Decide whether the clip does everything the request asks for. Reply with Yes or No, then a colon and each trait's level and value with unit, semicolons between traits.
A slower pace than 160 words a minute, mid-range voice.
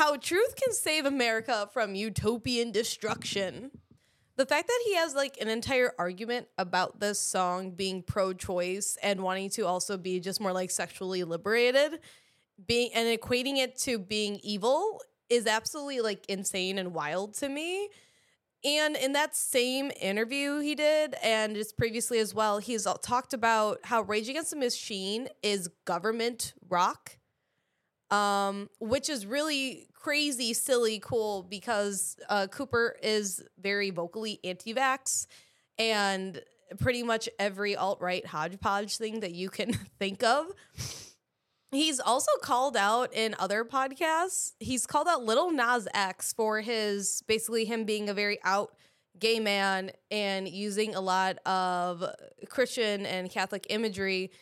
No: average, 145 wpm; high, 220 Hz